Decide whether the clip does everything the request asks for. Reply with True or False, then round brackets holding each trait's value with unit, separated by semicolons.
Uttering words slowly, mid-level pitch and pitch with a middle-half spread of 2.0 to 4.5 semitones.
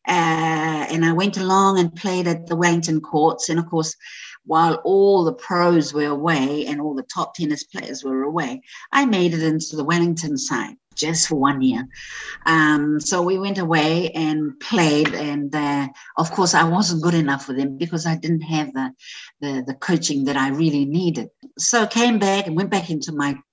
False (195 wpm; 160 Hz; 3.1 semitones)